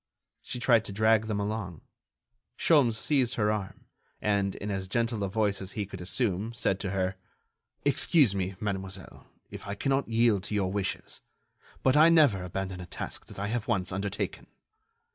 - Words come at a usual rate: Yes, average, 175 wpm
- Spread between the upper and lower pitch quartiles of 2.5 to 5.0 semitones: Yes, average, 3.2 semitones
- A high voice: No, low, 105 Hz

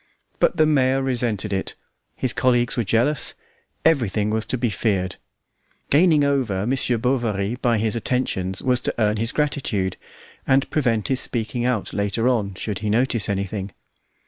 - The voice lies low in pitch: Yes, low, 115 Hz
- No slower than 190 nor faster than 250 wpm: No, average, 155 wpm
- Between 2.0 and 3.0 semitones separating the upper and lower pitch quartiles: No, average, 3.9 semitones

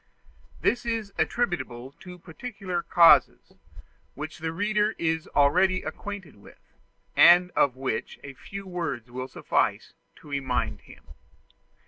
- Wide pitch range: Yes, wide, 5.7 semitones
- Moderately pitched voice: Yes, medium, 170 Hz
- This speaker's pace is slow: Yes, slow, 120 wpm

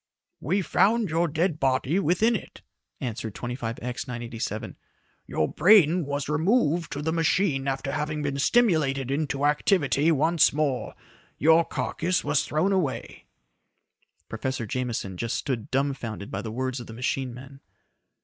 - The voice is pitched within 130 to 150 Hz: Yes, medium, 140 Hz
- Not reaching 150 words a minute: Yes, average, 140 wpm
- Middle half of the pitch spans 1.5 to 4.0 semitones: No, average, 4.4 semitones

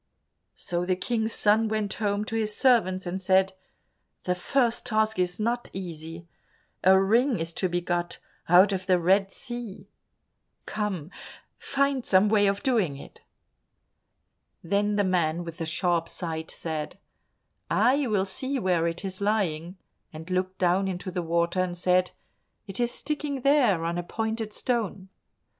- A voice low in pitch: No, high, 190 Hz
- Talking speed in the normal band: Yes, average, 155 wpm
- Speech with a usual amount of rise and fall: Yes, average, 3.8 semitones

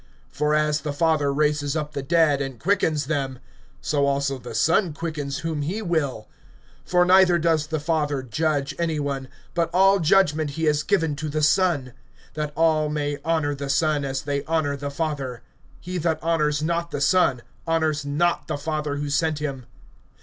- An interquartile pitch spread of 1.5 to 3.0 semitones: Yes, narrow, 2.4 semitones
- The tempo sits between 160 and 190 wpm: Yes, average, 180 wpm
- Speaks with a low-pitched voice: No, medium, 150 Hz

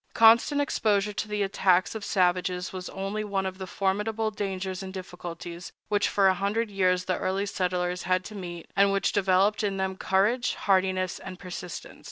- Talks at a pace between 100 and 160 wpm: No, average, 180 wpm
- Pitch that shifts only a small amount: Yes, narrow, 1.8 semitones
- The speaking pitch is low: No, high, 190 Hz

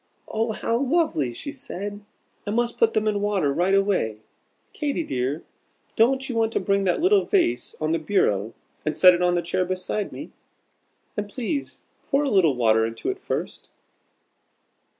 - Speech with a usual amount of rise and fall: No, wide, 6.5 semitones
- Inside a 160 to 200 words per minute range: Yes, average, 170 wpm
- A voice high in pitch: Yes, high, 205 Hz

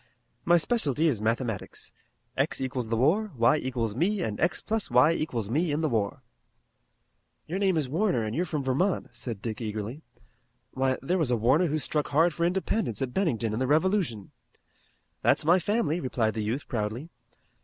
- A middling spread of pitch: No, wide, 6.7 semitones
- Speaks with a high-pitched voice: No, low, 135 Hz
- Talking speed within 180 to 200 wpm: Yes, average, 185 wpm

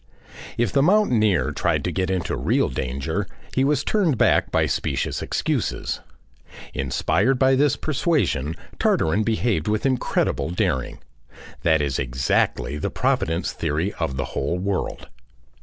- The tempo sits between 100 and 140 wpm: Yes, slow, 135 wpm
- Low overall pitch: Yes, very low, 95 Hz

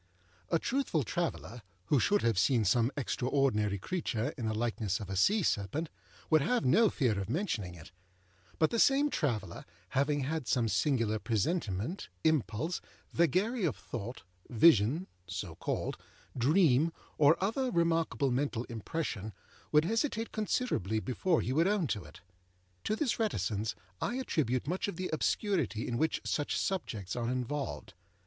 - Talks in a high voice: No, medium, 140 Hz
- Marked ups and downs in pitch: Yes, wide, 7.9 semitones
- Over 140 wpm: Yes, average, 150 wpm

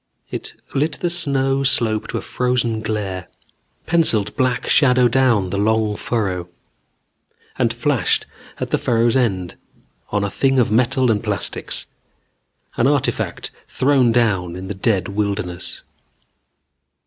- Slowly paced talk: Yes, slow, 130 wpm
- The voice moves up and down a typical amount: Yes, average, 4.2 semitones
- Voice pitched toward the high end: No, low, 115 Hz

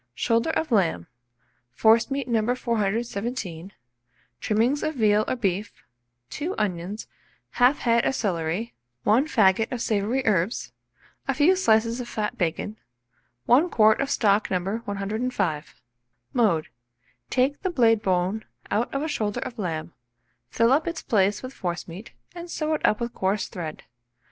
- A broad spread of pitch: No, average, 4.3 semitones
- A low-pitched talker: No, high, 220 Hz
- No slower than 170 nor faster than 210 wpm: No, average, 145 wpm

